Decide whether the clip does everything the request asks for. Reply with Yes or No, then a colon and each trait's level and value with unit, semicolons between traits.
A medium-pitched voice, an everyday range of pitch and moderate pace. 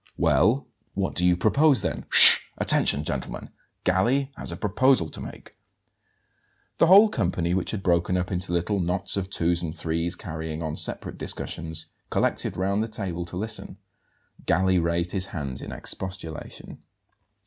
No: very low, 90 Hz; average, 3.2 semitones; average, 155 wpm